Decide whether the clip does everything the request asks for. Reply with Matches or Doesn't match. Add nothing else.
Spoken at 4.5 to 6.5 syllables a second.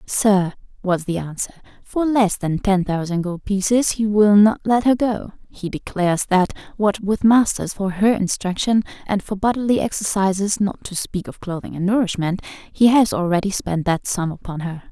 Matches